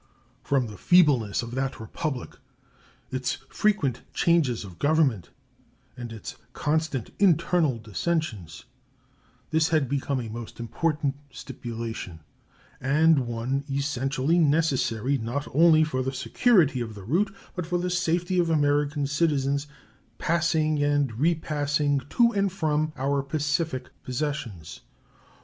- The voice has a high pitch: No, medium, 145 Hz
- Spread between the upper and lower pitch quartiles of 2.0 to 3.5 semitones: No, average, 4.2 semitones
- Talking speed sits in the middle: No, slow, 120 wpm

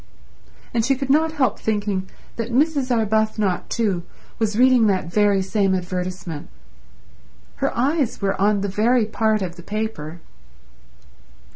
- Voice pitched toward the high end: Yes, high, 215 Hz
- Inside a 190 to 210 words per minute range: No, slow, 135 wpm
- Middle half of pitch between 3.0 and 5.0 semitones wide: Yes, average, 4.1 semitones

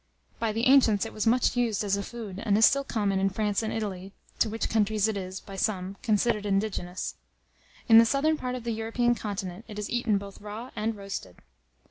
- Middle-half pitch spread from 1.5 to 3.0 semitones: Yes, narrow, 2.5 semitones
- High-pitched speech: Yes, high, 215 Hz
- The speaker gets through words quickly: Yes, fast, 210 wpm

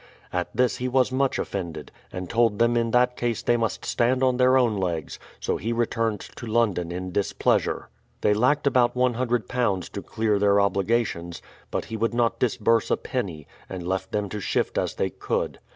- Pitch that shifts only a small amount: No, average, 4.0 semitones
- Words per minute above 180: Yes, average, 190 wpm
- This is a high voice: No, low, 115 Hz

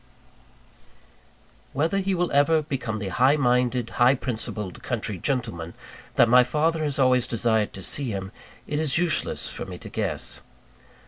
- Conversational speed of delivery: Yes, average, 150 wpm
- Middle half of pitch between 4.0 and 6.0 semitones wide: Yes, average, 4.9 semitones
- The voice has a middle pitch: No, low, 125 Hz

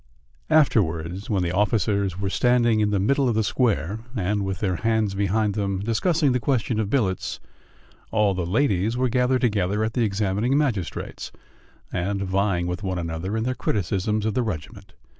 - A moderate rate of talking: Yes, average, 175 wpm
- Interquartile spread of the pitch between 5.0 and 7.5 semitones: No, average, 3.4 semitones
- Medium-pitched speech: No, low, 105 Hz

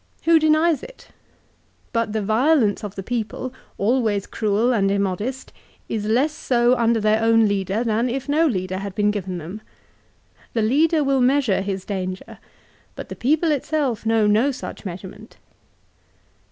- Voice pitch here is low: No, high, 225 Hz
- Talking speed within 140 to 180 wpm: Yes, average, 155 wpm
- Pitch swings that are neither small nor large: Yes, average, 4.6 semitones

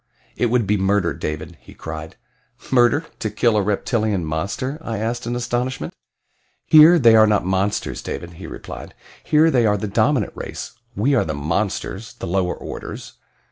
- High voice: No, low, 110 Hz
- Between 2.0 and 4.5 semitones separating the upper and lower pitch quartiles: Yes, average, 4.2 semitones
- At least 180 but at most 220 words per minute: No, average, 170 wpm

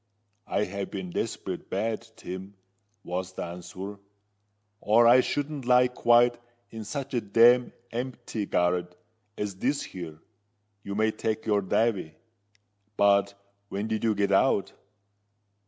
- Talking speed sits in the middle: No, slow, 130 wpm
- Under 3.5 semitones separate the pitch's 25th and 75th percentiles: No, average, 3.8 semitones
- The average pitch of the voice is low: Yes, low, 105 Hz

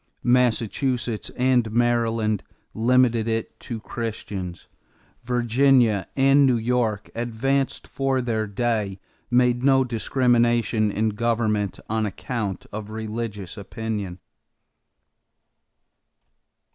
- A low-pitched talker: Yes, low, 115 Hz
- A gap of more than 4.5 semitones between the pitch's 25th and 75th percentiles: No, narrow, 2.4 semitones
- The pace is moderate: No, slow, 90 wpm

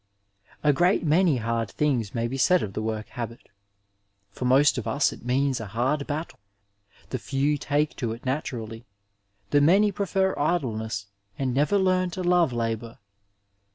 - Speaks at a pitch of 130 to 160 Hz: Yes, low, 135 Hz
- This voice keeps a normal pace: Yes, average, 160 wpm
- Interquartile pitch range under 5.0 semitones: No, wide, 5.4 semitones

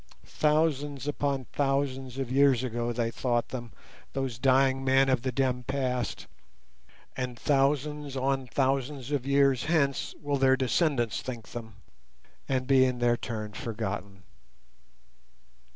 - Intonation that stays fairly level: Yes, narrow, 2.3 semitones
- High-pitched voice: No, low, 130 Hz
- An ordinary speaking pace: No, slow, 130 wpm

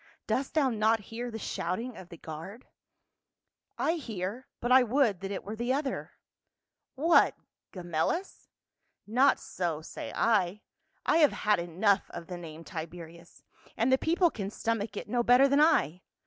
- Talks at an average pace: Yes, average, 160 wpm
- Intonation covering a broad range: Yes, wide, 6.4 semitones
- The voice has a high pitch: Yes, high, 215 Hz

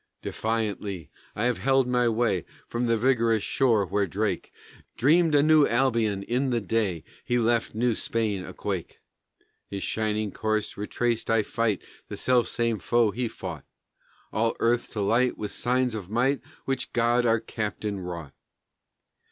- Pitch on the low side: Yes, low, 115 Hz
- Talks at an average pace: Yes, average, 155 wpm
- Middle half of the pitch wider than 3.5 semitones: No, narrow, 2.5 semitones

